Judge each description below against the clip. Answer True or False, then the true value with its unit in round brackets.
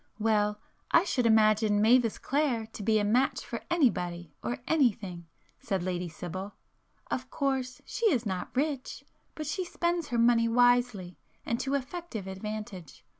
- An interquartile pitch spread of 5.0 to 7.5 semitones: False (4.6 semitones)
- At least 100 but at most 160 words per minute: True (135 wpm)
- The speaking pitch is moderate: False (230 Hz)